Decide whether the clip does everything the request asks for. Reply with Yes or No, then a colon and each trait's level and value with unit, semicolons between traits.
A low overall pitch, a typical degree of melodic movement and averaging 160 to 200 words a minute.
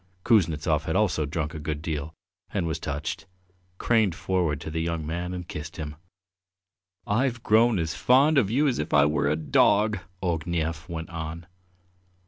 Yes: very low, 80 Hz; average, 3.9 semitones; average, 170 wpm